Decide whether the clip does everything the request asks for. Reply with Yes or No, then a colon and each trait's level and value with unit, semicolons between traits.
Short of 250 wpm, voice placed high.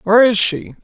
Yes: fast, 215 wpm; high, 205 Hz